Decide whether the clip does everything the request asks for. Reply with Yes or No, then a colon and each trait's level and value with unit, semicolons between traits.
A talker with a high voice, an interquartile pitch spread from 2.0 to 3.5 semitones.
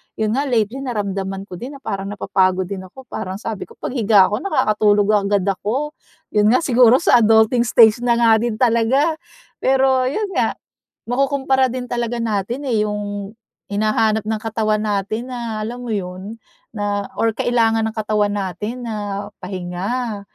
Yes: high, 220 Hz; average, 3.1 semitones